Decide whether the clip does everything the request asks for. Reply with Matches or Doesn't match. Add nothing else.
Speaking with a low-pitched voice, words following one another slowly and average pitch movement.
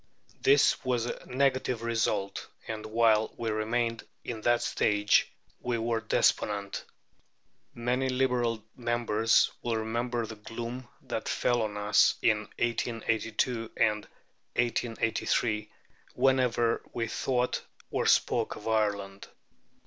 Doesn't match